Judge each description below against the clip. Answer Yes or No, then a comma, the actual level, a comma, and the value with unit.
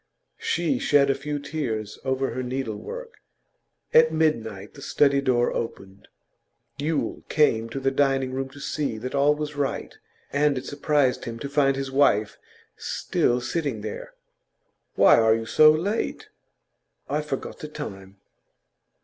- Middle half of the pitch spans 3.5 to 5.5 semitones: Yes, average, 3.8 semitones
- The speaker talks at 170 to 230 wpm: No, average, 145 wpm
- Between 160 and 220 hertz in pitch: No, low, 135 Hz